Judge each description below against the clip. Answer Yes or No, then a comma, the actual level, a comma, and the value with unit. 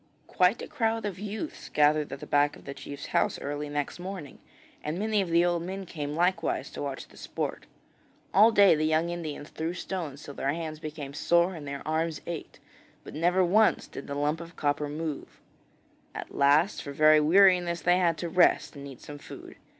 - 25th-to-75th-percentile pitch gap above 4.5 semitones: No, average, 3.5 semitones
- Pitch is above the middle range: No, medium, 160 Hz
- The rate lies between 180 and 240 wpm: Yes, average, 200 wpm